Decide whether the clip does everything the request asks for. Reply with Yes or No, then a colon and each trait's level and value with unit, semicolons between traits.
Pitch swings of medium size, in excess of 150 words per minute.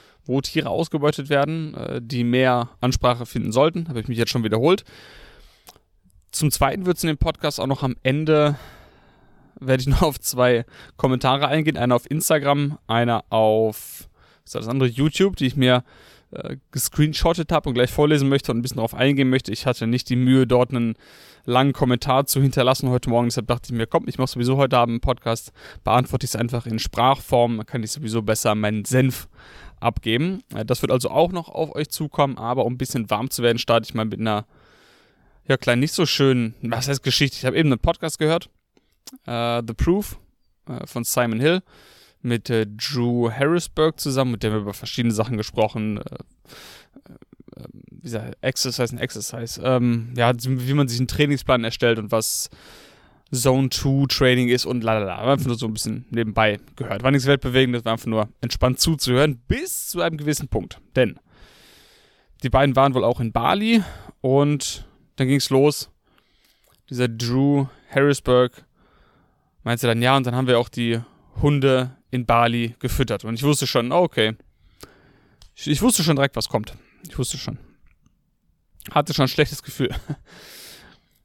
Yes: average, 3.2 semitones; average, 180 wpm